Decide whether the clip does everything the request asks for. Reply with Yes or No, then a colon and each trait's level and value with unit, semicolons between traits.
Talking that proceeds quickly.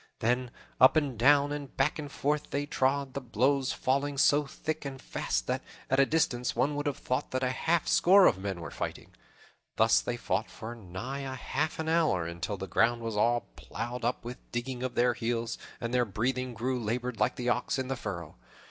Yes: fast, 210 wpm